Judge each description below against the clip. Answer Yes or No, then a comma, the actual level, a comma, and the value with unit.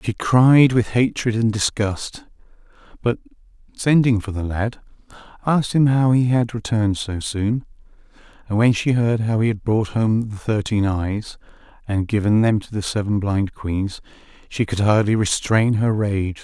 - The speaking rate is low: No, average, 165 wpm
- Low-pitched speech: Yes, low, 110 Hz